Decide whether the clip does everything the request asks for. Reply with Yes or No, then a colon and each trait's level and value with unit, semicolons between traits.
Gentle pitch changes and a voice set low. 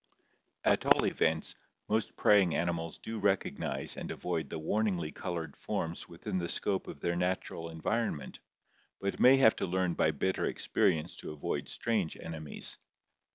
No: average, 3.6 semitones; very low, 90 Hz